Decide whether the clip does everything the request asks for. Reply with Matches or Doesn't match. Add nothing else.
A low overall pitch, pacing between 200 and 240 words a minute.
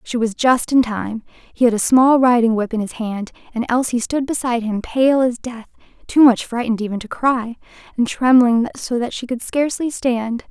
Doesn't match